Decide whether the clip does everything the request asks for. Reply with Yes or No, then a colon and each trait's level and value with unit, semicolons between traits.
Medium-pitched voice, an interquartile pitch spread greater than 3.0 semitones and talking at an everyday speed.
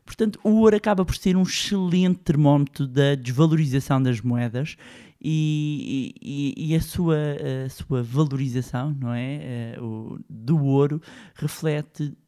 Yes: medium, 145 Hz; average, 3.4 semitones; average, 130 wpm